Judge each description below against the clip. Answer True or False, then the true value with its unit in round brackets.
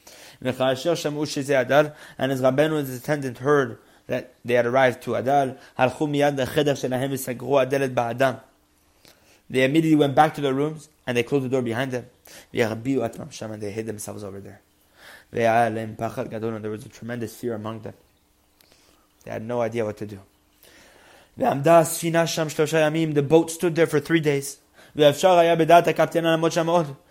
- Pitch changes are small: False (4.6 semitones)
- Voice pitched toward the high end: False (135 Hz)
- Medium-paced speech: False (120 wpm)